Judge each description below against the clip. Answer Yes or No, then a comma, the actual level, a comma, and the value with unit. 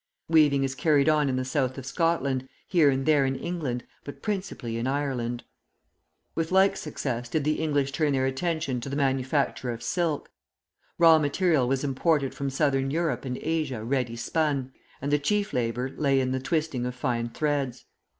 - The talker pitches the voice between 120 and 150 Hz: Yes, medium, 140 Hz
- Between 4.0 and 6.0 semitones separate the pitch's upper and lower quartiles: No, average, 3.3 semitones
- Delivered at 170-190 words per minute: Yes, average, 180 wpm